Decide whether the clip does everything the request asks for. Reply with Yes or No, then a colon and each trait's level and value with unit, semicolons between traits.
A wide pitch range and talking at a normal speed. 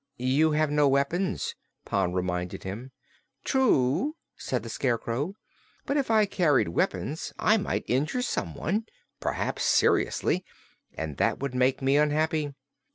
No: wide, 6.0 semitones; slow, 130 wpm